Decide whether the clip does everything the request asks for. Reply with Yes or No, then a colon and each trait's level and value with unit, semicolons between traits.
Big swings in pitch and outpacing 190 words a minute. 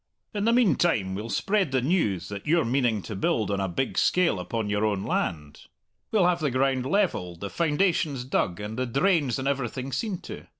Yes: wide, 8.6 semitones; average, 200 wpm